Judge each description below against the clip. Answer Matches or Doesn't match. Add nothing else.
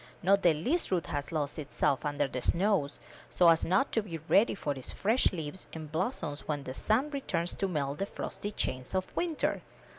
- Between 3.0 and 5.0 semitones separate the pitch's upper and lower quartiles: Doesn't match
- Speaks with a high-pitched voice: Doesn't match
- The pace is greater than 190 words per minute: Matches